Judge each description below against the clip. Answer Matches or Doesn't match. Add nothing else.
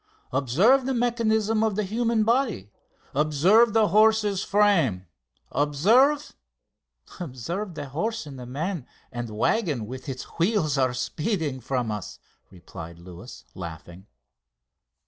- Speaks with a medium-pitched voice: Matches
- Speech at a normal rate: Doesn't match